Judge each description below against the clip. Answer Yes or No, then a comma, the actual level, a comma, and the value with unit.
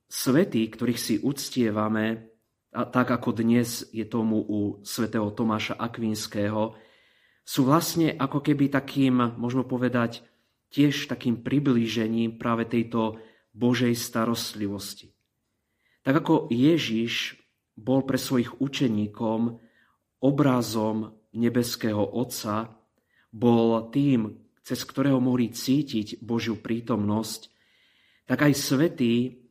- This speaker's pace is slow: Yes, slow, 100 wpm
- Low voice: Yes, low, 115 Hz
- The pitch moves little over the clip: Yes, narrow, 2.1 semitones